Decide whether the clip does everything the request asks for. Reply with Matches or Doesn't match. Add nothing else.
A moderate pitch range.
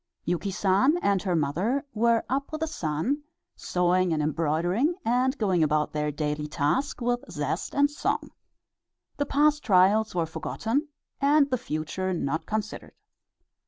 Doesn't match